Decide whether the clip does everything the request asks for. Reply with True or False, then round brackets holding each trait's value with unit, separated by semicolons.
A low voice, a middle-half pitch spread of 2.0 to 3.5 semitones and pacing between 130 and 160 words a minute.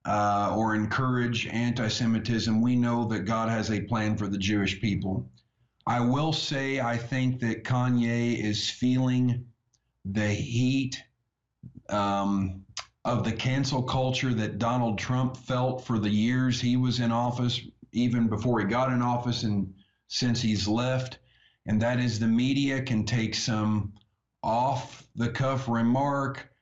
True (120 Hz; 2.6 semitones; 145 wpm)